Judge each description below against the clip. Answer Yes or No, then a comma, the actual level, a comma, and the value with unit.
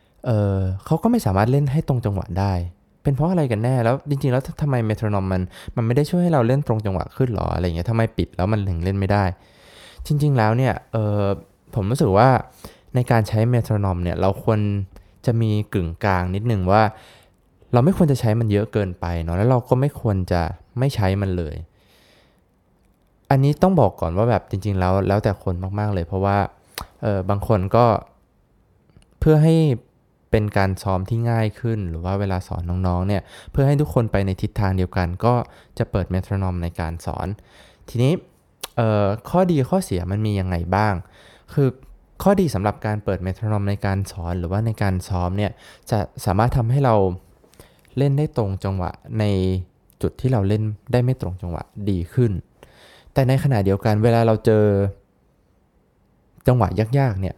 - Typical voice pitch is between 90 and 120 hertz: Yes, low, 105 Hz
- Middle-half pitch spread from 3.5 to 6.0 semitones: Yes, average, 4.3 semitones